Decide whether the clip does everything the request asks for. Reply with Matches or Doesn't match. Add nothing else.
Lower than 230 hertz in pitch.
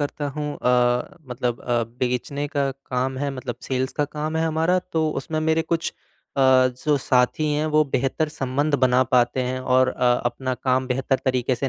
Matches